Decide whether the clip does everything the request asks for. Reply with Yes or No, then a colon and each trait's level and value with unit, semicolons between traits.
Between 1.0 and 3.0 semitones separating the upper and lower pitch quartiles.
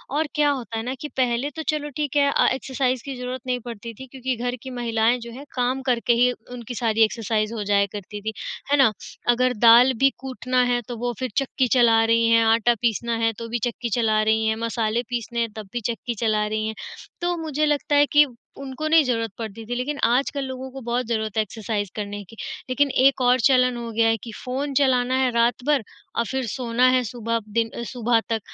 Yes: narrow, 2.4 semitones